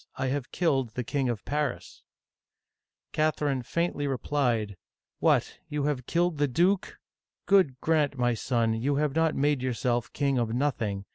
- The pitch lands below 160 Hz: Yes, medium, 140 Hz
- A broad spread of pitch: No, average, 3.7 semitones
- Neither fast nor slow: Yes, average, 160 wpm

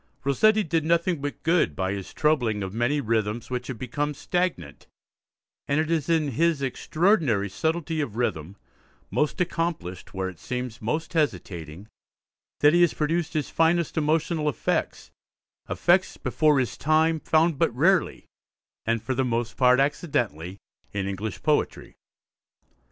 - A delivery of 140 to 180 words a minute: Yes, average, 145 wpm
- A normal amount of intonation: No, wide, 6.5 semitones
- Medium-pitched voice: Yes, medium, 145 Hz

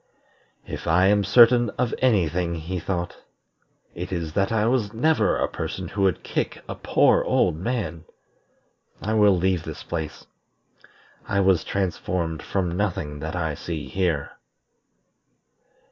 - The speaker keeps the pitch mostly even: No, average, 3.8 semitones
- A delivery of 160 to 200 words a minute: No, average, 145 wpm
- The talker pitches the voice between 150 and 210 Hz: No, very low, 95 Hz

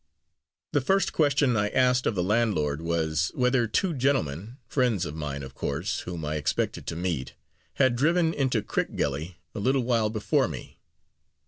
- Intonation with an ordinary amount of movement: No, wide, 8.3 semitones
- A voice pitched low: Yes, low, 110 Hz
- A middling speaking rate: Yes, average, 160 wpm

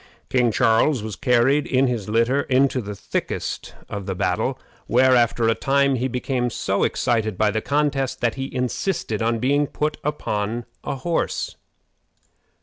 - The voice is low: Yes, low, 125 Hz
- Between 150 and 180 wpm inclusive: Yes, average, 155 wpm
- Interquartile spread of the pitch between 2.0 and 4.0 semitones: Yes, average, 3.3 semitones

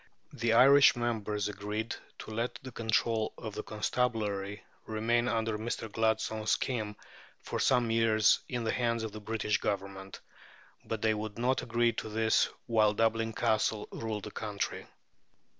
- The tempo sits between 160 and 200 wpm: No, average, 150 wpm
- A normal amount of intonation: No, narrow, 1.6 semitones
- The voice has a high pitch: No, low, 110 Hz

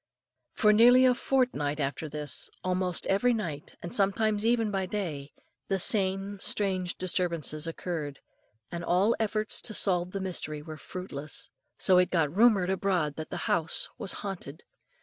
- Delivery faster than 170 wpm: No, average, 150 wpm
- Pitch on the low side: No, medium, 185 Hz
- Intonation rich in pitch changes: No, average, 4.4 semitones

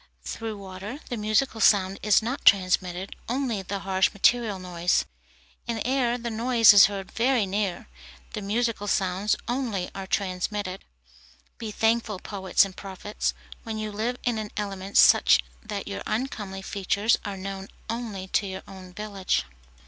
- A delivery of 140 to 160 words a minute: Yes, average, 150 wpm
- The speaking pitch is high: Yes, high, 205 Hz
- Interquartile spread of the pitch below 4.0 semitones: Yes, average, 2.9 semitones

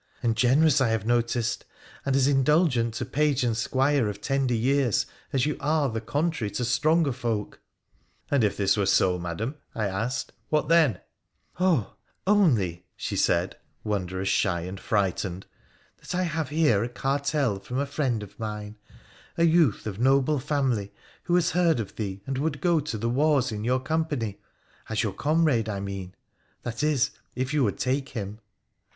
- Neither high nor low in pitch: No, low, 125 Hz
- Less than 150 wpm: No, average, 185 wpm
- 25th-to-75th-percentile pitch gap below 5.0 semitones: No, wide, 5.6 semitones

